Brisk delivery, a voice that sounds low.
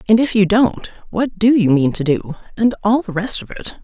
No: fast, 250 wpm; high, 200 Hz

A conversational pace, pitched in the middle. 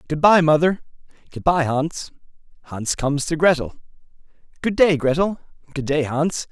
No: slow, 130 wpm; medium, 155 Hz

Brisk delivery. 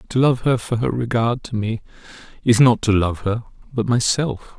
No: average, 195 wpm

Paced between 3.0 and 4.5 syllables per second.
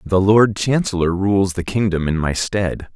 Yes: 4.2 syllables/s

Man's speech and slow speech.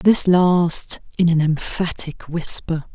No: female; slow, 120 wpm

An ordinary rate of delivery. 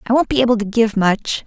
No: fast, 285 wpm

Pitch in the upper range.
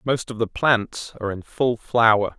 No: low, 115 Hz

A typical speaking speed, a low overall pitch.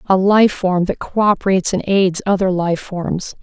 No: average, 175 wpm; high, 190 Hz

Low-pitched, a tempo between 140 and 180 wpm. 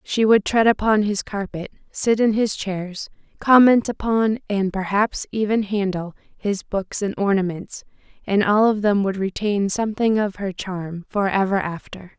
No: high, 205 Hz; average, 160 wpm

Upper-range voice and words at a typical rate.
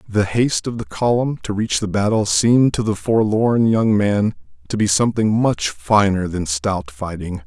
No: low, 105 Hz; average, 185 wpm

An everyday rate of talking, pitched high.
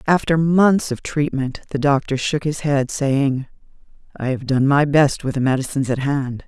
No: average, 185 wpm; medium, 140 Hz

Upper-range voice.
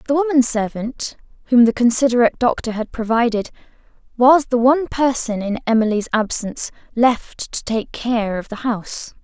Yes: high, 235 Hz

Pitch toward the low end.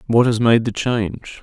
Yes: low, 115 Hz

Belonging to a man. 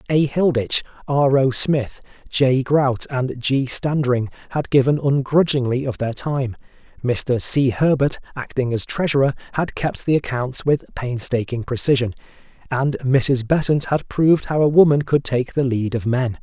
Yes: male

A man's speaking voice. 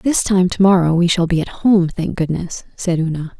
No: female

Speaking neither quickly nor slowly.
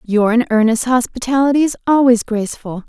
Yes: average, 145 wpm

